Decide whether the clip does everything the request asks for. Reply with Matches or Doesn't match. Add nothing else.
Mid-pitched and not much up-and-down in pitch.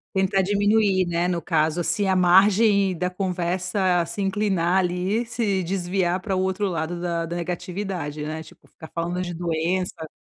Matches